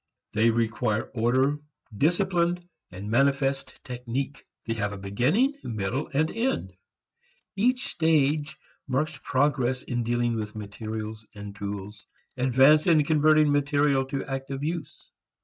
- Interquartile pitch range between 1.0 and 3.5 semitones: No, average, 5.1 semitones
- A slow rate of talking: Yes, slow, 120 wpm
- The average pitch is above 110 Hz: Yes, low, 135 Hz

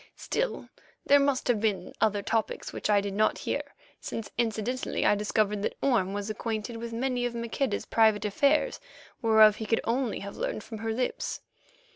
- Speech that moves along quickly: No, average, 175 wpm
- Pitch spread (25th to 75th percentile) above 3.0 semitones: No, narrow, 2.6 semitones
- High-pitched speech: Yes, high, 225 Hz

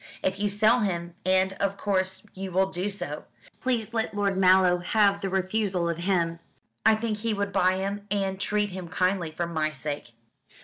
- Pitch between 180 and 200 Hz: Yes, high, 190 Hz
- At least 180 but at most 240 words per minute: Yes, average, 185 wpm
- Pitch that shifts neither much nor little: No, narrow, 2.3 semitones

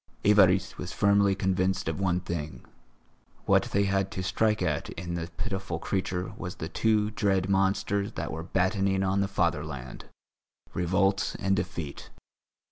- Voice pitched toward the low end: Yes, very low, 95 Hz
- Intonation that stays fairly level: Yes, narrow, 2.1 semitones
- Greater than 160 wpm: No, average, 145 wpm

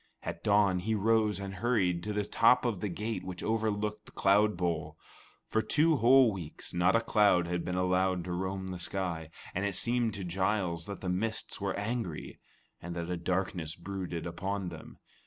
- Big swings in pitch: No, average, 3.3 semitones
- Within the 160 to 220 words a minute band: Yes, average, 190 wpm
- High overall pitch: No, very low, 95 Hz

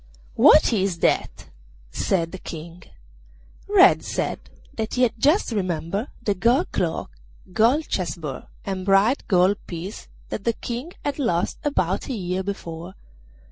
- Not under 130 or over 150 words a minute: Yes, average, 140 wpm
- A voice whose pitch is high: Yes, high, 195 Hz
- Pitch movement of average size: Yes, average, 5.0 semitones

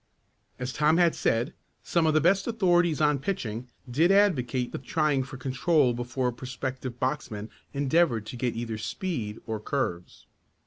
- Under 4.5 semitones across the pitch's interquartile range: No, average, 4.9 semitones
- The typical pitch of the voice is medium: No, low, 130 Hz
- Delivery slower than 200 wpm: Yes, average, 155 wpm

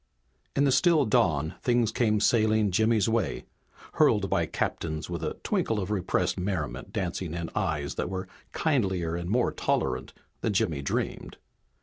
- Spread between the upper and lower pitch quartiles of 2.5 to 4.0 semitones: No, average, 4.9 semitones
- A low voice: Yes, low, 100 Hz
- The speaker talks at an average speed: Yes, average, 150 wpm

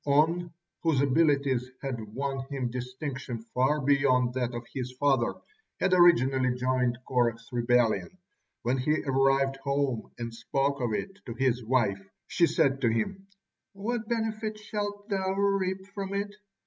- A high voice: No, low, 135 Hz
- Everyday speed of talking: Yes, average, 145 wpm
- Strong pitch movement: Yes, wide, 6.0 semitones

